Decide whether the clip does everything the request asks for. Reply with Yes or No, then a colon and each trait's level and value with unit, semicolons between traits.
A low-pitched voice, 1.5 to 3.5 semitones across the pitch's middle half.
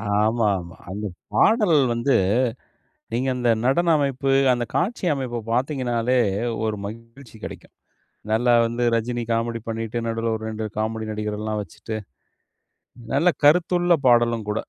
Yes: low, 115 Hz; average, 3.1 semitones